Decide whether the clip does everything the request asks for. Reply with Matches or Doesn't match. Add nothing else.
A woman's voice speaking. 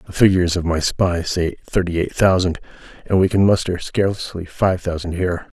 Doesn't match